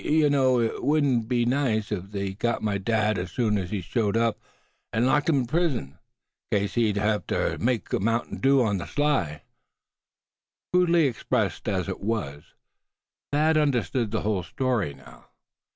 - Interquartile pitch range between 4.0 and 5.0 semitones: Yes, average, 4.7 semitones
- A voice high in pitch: No, low, 115 Hz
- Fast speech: No, average, 175 wpm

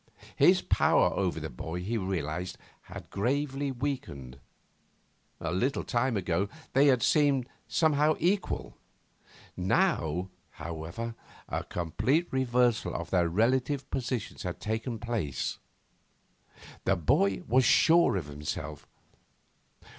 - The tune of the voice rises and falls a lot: Yes, wide, 7.4 semitones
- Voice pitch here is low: Yes, low, 110 Hz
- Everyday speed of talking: No, slow, 110 wpm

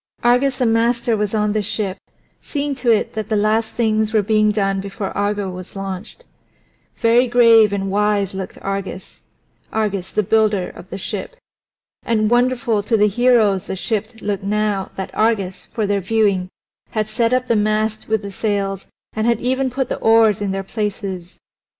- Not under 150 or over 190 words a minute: Yes, average, 175 wpm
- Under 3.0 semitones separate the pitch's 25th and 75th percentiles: Yes, narrow, 2.4 semitones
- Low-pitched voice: No, high, 215 Hz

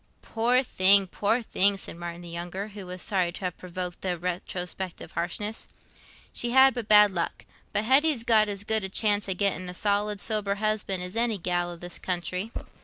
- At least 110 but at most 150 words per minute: No, average, 185 wpm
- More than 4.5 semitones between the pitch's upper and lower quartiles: No, average, 3.0 semitones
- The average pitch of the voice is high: Yes, high, 195 Hz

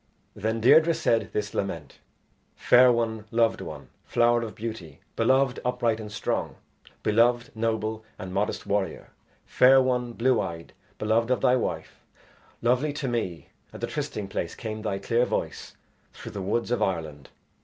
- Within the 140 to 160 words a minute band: Yes, average, 155 wpm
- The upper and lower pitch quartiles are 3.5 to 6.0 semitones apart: No, average, 2.8 semitones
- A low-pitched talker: Yes, low, 115 Hz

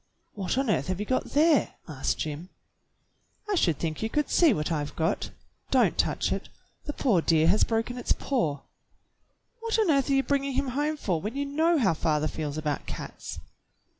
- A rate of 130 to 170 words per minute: No, average, 195 wpm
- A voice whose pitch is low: No, high, 220 Hz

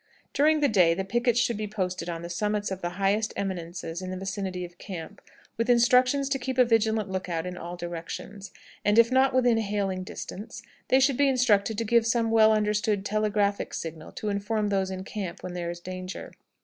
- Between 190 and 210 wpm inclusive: Yes, average, 200 wpm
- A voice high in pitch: Yes, high, 205 Hz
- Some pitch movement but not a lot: Yes, average, 3.8 semitones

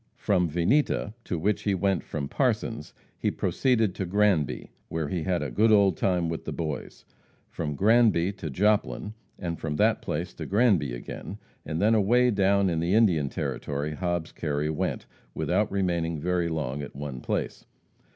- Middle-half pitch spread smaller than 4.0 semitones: No, average, 4.4 semitones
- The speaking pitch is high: No, very low, 90 Hz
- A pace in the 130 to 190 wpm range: Yes, average, 165 wpm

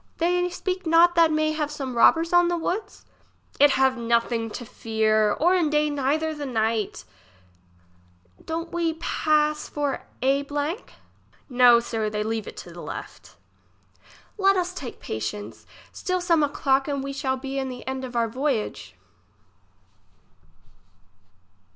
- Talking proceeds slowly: No, average, 145 wpm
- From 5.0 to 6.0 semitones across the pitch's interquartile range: Yes, wide, 5.6 semitones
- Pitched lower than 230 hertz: No, very high, 280 Hz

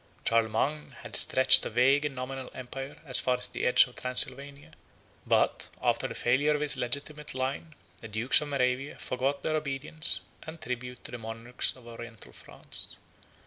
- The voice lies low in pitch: Yes, low, 130 Hz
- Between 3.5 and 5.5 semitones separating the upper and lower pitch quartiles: No, narrow, 2.5 semitones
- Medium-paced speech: Yes, average, 170 wpm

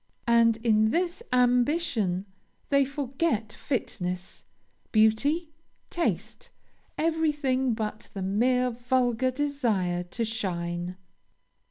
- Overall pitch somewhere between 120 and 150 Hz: No, high, 240 Hz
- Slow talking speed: Yes, slow, 85 wpm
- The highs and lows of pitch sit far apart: No, average, 4.8 semitones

